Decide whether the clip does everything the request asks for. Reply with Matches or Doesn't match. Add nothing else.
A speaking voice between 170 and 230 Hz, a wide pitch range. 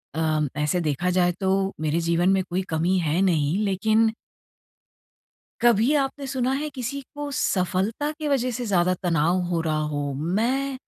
Matches